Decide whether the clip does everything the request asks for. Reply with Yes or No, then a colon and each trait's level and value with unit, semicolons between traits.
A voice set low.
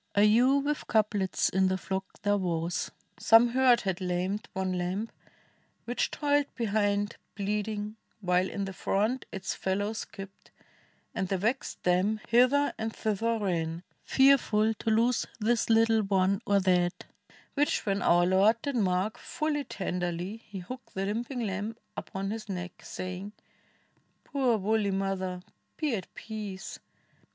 No: high, 205 Hz